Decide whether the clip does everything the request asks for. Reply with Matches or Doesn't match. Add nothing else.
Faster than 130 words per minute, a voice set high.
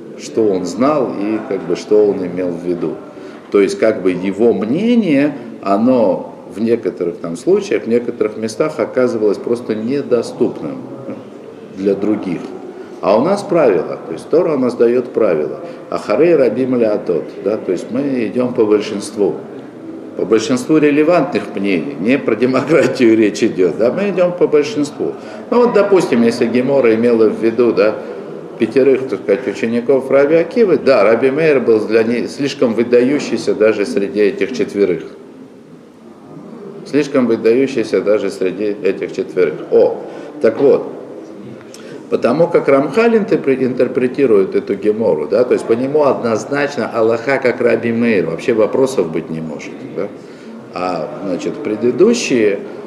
Doesn't match